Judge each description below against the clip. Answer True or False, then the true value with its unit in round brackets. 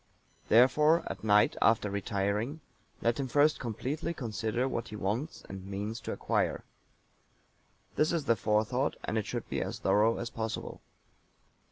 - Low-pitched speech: True (115 Hz)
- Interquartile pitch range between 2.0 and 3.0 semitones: False (4.2 semitones)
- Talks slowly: False (150 wpm)